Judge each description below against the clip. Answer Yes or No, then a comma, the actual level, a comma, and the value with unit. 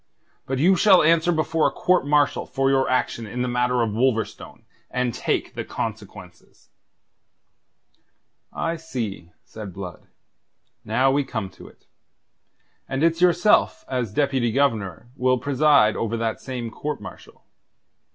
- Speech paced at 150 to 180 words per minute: No, average, 140 wpm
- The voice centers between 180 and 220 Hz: No, low, 130 Hz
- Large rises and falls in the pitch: No, average, 4.7 semitones